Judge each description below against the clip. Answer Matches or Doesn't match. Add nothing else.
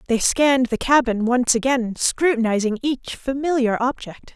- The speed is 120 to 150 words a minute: Matches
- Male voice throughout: Doesn't match